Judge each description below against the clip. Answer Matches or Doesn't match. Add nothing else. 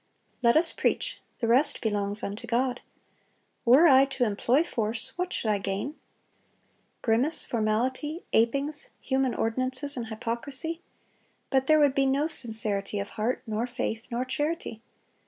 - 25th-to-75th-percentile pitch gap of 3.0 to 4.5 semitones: Matches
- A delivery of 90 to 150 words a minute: Matches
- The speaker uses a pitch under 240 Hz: Doesn't match